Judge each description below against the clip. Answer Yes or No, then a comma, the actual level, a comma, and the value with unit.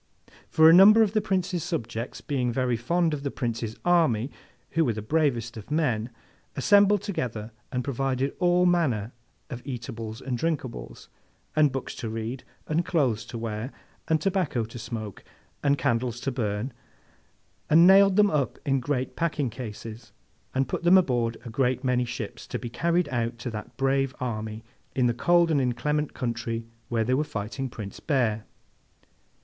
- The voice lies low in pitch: Yes, low, 130 Hz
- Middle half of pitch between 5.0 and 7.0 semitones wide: Yes, wide, 5.4 semitones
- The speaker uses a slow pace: No, average, 165 wpm